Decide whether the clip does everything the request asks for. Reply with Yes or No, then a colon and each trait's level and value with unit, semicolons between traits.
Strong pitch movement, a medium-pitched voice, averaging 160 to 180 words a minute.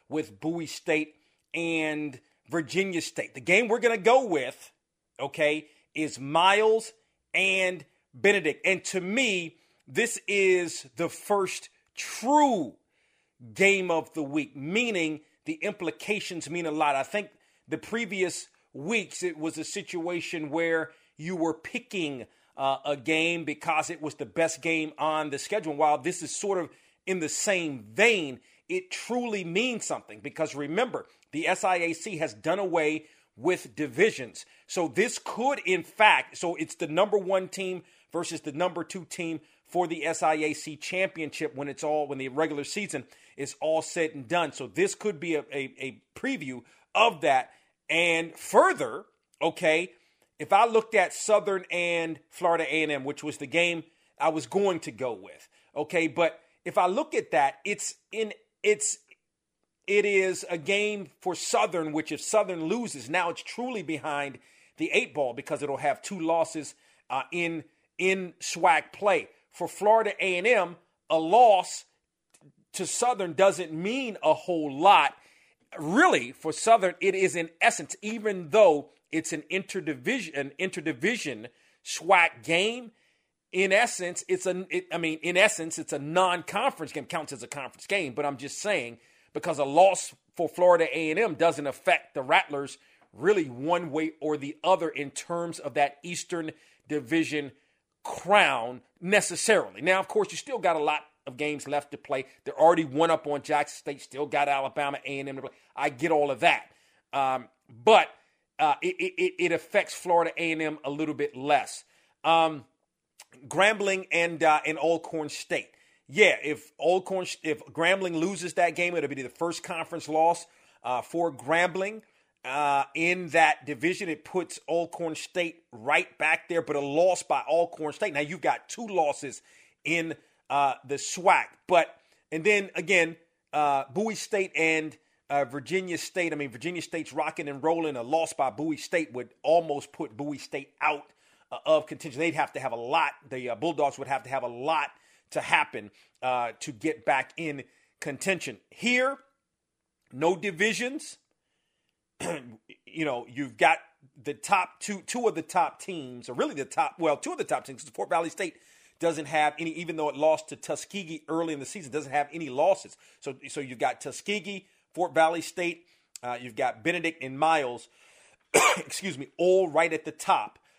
No: average, 3.8 semitones; medium, 165 Hz; average, 165 wpm